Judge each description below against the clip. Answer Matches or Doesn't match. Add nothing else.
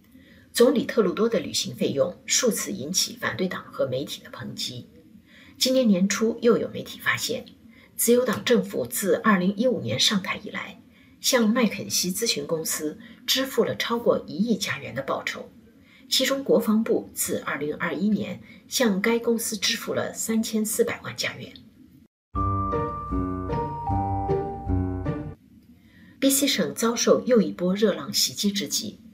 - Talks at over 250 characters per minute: Doesn't match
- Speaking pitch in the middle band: Doesn't match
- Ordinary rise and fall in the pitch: Doesn't match